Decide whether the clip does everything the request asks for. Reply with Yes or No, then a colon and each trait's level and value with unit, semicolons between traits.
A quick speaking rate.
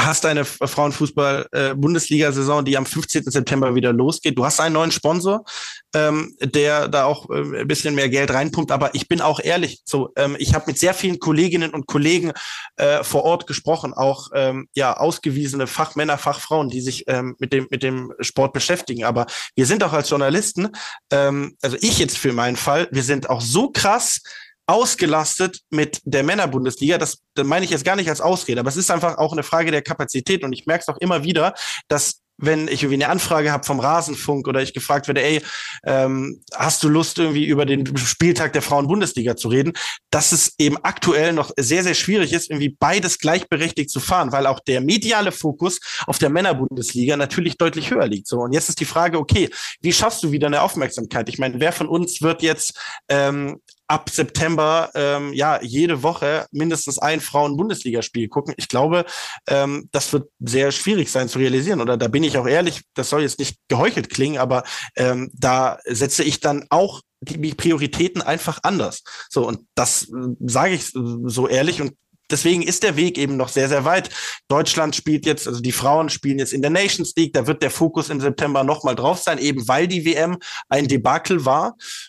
Yes: fast, 195 wpm